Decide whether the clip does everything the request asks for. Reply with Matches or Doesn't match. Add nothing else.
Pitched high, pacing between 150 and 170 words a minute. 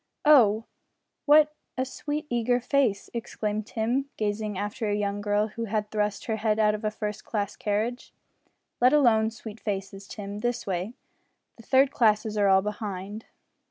Matches